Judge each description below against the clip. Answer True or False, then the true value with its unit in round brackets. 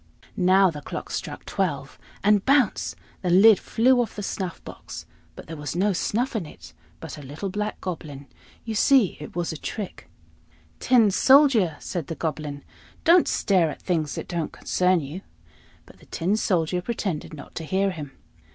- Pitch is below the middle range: False (185 Hz)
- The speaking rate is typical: True (175 wpm)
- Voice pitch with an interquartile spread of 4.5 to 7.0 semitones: True (5.0 semitones)